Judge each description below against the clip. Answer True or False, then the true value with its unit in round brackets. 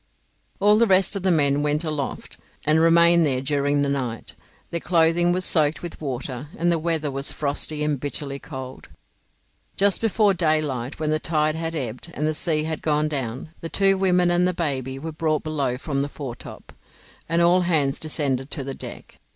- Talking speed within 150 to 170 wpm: False (190 wpm)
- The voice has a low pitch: False (155 Hz)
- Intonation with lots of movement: False (3.3 semitones)